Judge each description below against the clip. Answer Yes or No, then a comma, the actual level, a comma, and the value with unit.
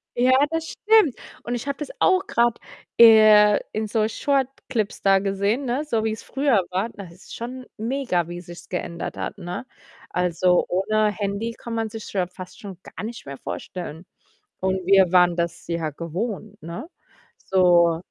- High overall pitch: Yes, high, 210 Hz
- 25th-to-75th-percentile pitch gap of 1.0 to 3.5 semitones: No, average, 4.8 semitones